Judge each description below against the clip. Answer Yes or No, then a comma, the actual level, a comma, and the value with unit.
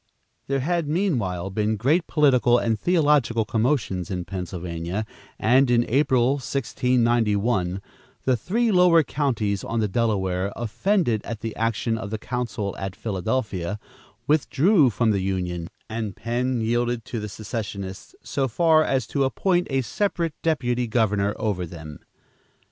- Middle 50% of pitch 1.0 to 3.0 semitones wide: No, average, 5.0 semitones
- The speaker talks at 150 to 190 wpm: No, slow, 135 wpm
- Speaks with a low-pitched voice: Yes, low, 115 Hz